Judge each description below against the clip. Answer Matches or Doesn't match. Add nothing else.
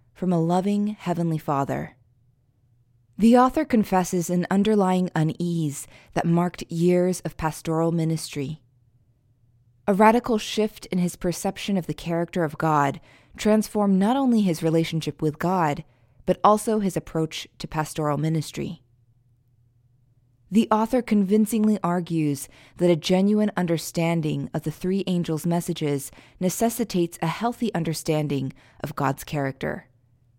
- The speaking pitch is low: Doesn't match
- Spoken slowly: Matches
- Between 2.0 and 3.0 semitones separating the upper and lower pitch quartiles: Doesn't match